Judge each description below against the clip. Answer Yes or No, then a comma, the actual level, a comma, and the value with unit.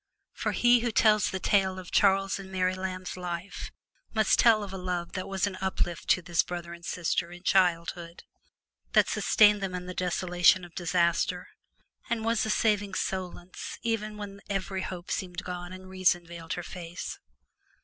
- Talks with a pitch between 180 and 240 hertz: Yes, medium, 185 Hz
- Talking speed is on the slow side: No, average, 175 wpm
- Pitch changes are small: Yes, narrow, 2.1 semitones